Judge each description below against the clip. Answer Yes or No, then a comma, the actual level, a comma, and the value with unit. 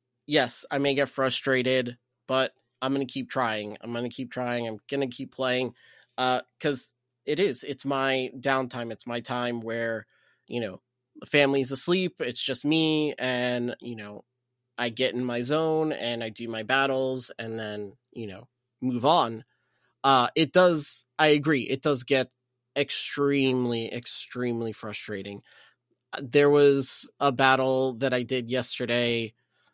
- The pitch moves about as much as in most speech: No, narrow, 2.1 semitones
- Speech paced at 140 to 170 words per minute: Yes, average, 155 wpm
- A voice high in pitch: No, low, 125 Hz